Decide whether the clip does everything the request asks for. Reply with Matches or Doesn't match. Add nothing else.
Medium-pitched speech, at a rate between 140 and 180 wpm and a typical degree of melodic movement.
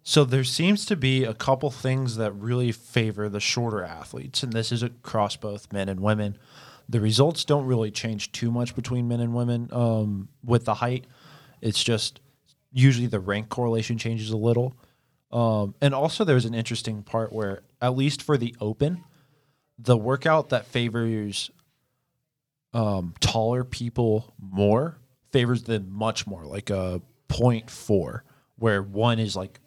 Doesn't match